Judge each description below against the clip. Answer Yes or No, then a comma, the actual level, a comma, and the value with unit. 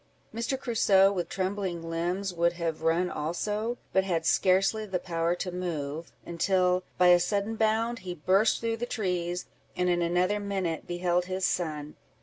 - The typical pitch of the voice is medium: Yes, medium, 180 Hz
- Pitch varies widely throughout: No, average, 2.7 semitones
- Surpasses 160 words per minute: No, average, 155 wpm